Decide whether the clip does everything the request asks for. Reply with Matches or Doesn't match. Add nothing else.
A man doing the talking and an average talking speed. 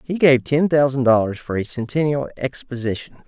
Matches